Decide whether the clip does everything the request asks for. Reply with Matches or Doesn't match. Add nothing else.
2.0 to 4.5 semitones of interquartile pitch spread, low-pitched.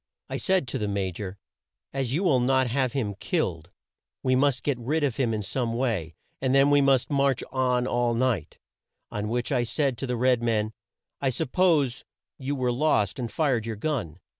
Matches